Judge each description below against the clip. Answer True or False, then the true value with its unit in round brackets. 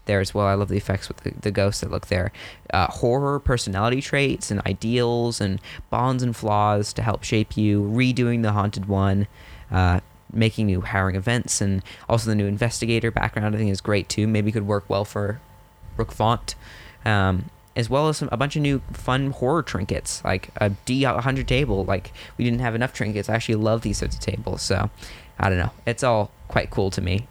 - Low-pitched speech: True (105 Hz)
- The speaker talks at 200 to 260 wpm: True (205 wpm)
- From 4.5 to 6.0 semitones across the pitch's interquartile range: False (3.3 semitones)